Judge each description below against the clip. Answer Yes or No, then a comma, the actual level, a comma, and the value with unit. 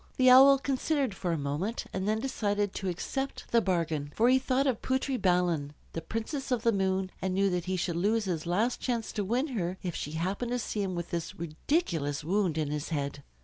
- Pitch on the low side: No, high, 195 Hz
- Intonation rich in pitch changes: Yes, wide, 6.2 semitones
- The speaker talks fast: Yes, fast, 220 wpm